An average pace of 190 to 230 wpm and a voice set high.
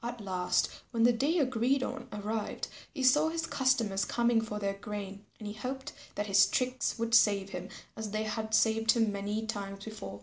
Yes: average, 195 wpm; high, 220 Hz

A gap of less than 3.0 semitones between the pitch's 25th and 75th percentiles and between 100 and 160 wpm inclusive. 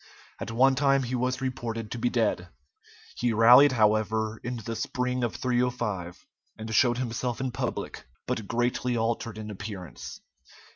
Yes: narrow, 2.5 semitones; average, 150 wpm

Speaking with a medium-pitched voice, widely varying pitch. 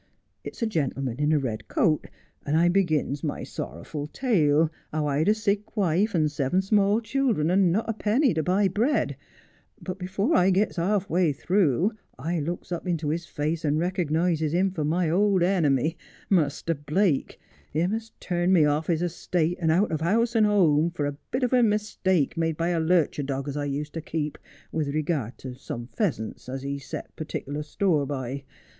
No: medium, 165 Hz; average, 4.6 semitones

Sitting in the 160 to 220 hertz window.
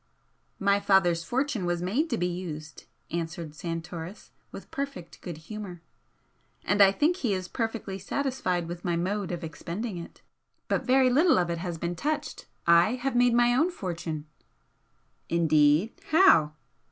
Yes: medium, 185 Hz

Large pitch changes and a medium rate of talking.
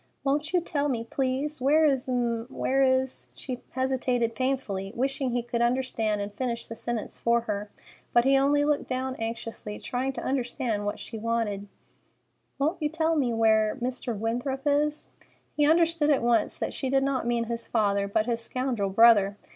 No: average, 3.1 semitones; average, 165 wpm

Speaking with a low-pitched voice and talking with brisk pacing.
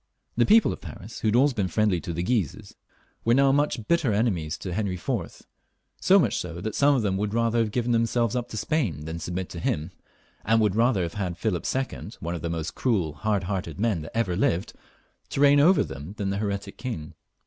Yes: low, 105 Hz; fast, 215 wpm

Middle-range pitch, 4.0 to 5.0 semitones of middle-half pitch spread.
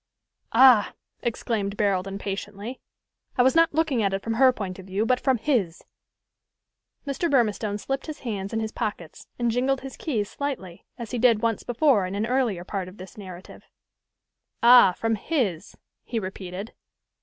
No: high, 220 Hz; average, 4.5 semitones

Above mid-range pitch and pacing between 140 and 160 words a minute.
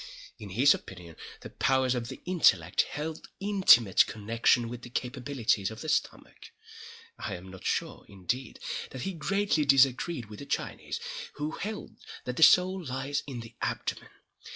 No: low, 130 Hz; average, 155 wpm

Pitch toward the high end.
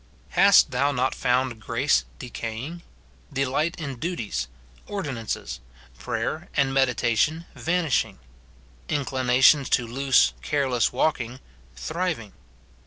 No: low, 135 Hz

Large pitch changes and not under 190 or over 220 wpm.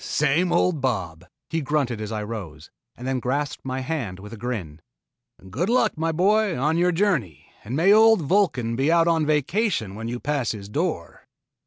Yes: wide, 7.0 semitones; average, 195 wpm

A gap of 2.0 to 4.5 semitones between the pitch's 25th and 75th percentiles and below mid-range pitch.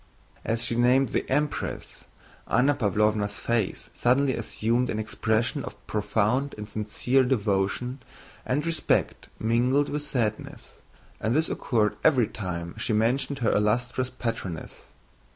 Yes: average, 3.5 semitones; low, 115 Hz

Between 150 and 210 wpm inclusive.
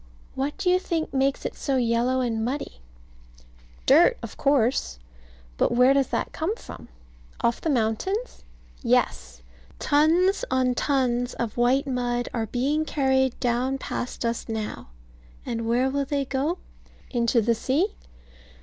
No: average, 140 wpm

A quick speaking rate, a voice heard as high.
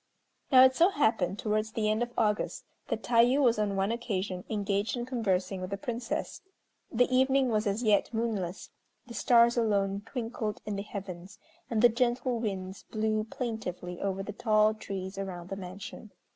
No: average, 170 wpm; high, 215 Hz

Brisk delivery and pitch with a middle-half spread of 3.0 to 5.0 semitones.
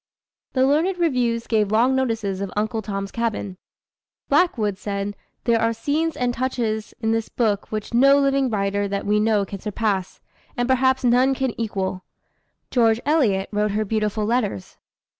No: average, 160 wpm; average, 3.7 semitones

